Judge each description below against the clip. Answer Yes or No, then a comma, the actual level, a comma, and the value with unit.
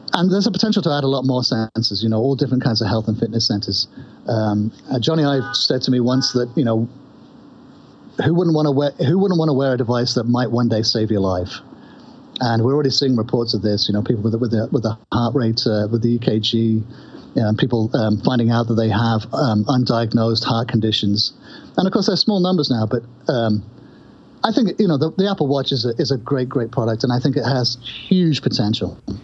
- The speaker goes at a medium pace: No, fast, 230 wpm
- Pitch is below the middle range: Yes, low, 125 Hz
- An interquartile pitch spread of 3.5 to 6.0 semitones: Yes, average, 4.2 semitones